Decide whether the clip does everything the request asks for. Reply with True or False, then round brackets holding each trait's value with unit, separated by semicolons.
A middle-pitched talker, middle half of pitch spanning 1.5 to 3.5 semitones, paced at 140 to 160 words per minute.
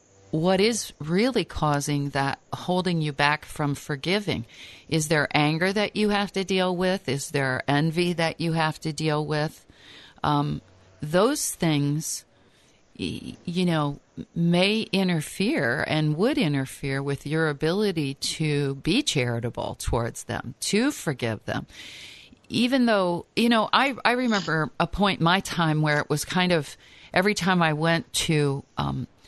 False (160 Hz; 4.5 semitones; 150 wpm)